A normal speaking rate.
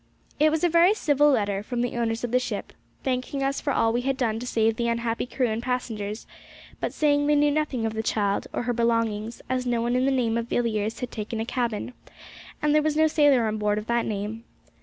No: fast, 240 wpm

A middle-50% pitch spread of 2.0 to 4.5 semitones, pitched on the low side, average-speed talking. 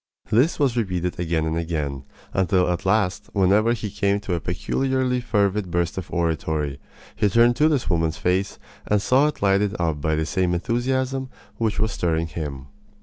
No: wide, 5.5 semitones; very low, 95 Hz; average, 175 wpm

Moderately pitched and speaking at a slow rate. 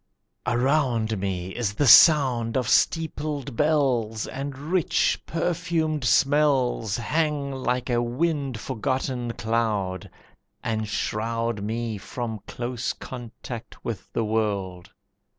No: low, 120 Hz; slow, 105 wpm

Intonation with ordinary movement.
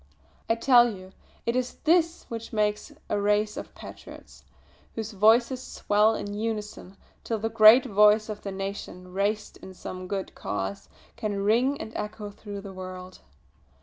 No: narrow, 2.3 semitones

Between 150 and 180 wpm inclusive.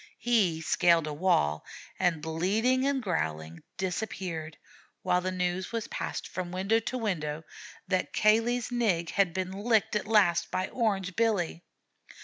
No: average, 140 wpm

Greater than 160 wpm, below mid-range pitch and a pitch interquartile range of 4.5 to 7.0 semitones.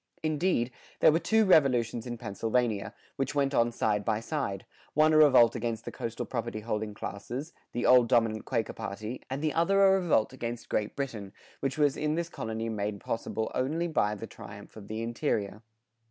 Yes: average, 185 wpm; low, 120 Hz; average, 5.1 semitones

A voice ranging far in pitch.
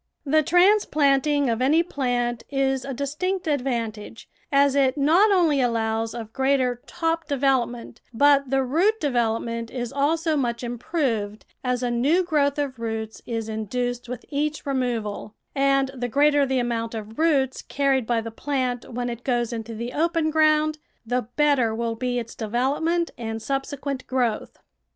No: average, 3.6 semitones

